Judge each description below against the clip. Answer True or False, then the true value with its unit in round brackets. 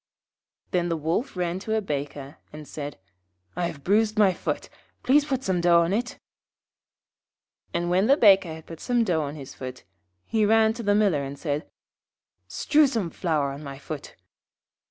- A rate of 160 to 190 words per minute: True (175 wpm)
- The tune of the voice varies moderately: False (6.3 semitones)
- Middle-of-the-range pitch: True (175 Hz)